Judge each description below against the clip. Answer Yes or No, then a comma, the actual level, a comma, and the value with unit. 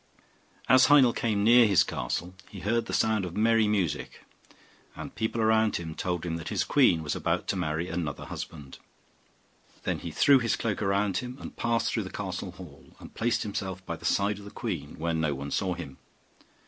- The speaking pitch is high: No, low, 100 Hz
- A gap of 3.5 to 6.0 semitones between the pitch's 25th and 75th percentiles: Yes, average, 4.6 semitones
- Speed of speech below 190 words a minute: No, average, 200 wpm